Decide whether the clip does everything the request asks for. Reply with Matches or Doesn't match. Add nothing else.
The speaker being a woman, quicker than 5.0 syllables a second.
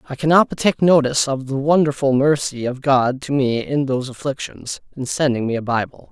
Doesn't match